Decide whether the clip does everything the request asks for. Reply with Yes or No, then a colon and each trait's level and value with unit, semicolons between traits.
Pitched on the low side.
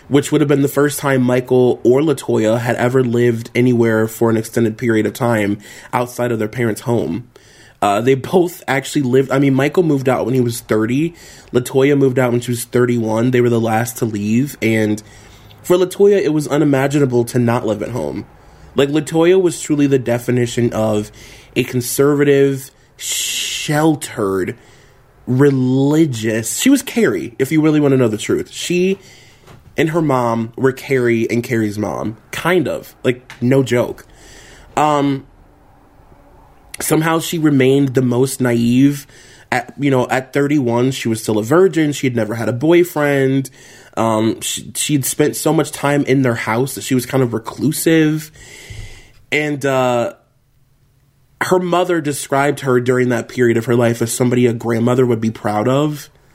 Yes: low, 130 Hz